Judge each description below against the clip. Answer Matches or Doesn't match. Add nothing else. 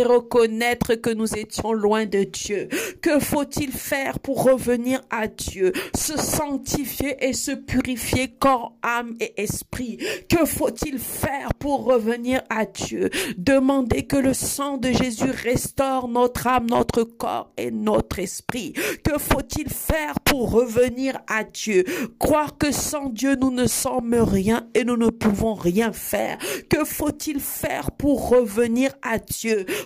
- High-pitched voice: Matches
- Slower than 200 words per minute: Matches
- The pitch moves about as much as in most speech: Matches